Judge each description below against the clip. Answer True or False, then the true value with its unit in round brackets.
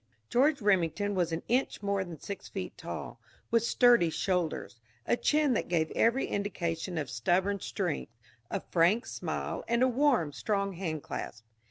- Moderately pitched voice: False (195 Hz)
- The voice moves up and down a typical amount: False (5.8 semitones)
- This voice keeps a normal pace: True (155 wpm)